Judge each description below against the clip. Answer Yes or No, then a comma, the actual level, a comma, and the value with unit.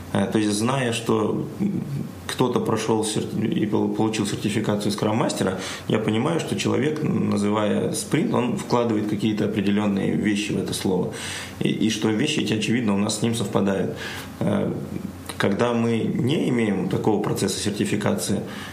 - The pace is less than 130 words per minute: No, average, 135 wpm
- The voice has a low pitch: Yes, low, 105 Hz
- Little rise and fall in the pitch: Yes, narrow, 1.1 semitones